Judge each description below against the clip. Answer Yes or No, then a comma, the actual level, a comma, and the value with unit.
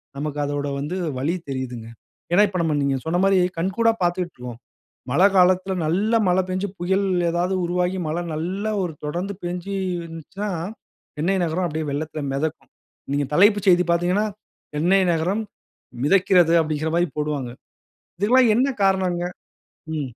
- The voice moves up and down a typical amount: Yes, average, 3.7 semitones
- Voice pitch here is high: No, medium, 175 Hz